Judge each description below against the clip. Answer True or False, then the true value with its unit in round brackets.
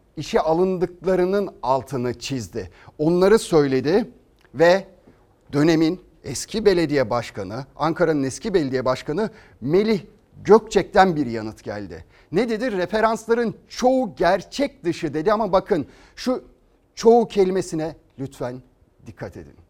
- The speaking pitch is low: False (165 Hz)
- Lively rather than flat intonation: True (7.5 semitones)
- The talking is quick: False (105 wpm)